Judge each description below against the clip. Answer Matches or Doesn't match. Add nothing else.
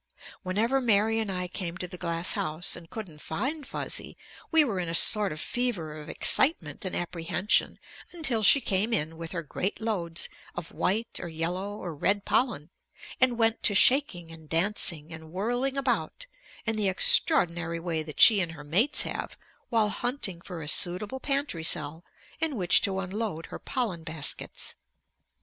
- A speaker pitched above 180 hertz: Matches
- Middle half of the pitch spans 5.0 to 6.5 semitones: Matches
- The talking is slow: Doesn't match